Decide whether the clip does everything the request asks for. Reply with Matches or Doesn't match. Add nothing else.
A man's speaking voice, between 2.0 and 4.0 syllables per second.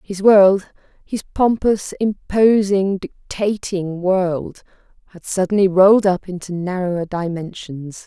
Doesn't match